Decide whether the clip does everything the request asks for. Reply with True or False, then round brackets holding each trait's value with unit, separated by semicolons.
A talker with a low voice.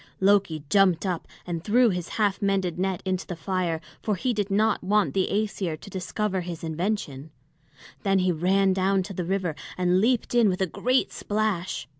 False (190 Hz)